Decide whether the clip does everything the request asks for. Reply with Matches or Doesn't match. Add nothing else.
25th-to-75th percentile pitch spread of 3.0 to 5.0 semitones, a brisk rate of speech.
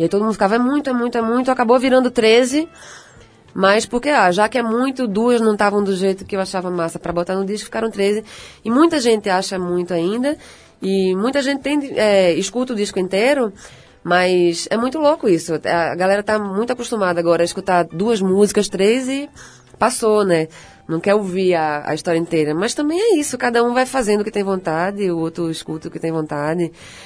Doesn't match